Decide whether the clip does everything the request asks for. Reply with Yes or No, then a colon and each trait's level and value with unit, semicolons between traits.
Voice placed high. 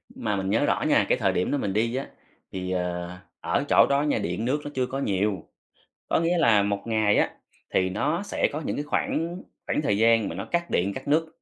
No: low, 115 Hz